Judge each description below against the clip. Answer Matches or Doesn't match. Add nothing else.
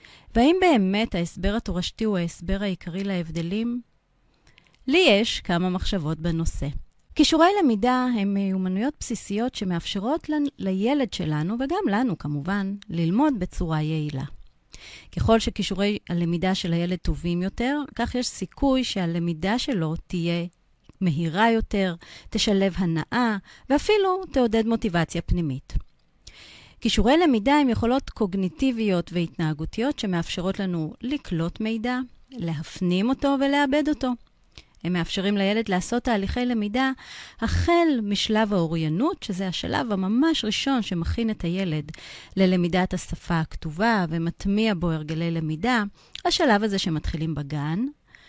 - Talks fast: Doesn't match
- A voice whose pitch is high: Matches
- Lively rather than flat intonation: Matches